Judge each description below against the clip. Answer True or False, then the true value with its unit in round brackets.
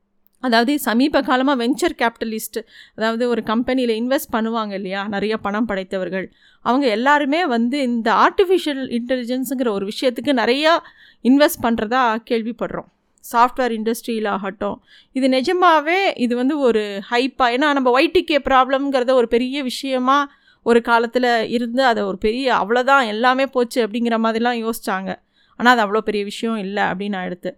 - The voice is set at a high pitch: True (240 Hz)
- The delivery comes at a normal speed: False (135 wpm)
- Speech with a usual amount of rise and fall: True (3.3 semitones)